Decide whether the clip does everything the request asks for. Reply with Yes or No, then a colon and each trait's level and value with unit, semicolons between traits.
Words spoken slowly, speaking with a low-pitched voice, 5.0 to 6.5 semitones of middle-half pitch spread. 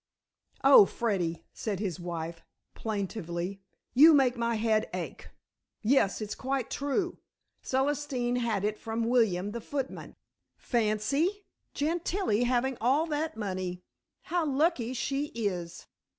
No: slow, 120 wpm; high, 235 Hz; average, 5.3 semitones